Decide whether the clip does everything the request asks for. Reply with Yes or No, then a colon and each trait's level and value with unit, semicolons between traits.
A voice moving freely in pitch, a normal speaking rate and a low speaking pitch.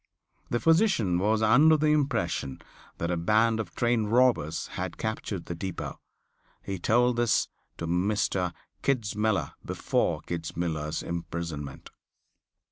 No: wide, 5.8 semitones; slow, 120 wpm; low, 105 Hz